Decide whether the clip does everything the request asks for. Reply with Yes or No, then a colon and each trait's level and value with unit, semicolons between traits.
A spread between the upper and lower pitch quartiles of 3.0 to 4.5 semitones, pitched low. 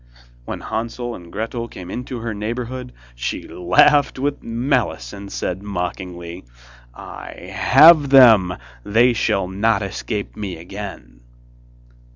No: average, 5.1 semitones; low, 105 Hz